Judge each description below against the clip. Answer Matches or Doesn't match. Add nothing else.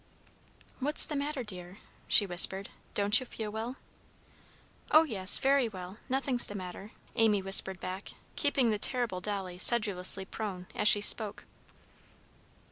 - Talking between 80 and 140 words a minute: Matches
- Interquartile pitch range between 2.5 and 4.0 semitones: Doesn't match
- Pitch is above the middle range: Matches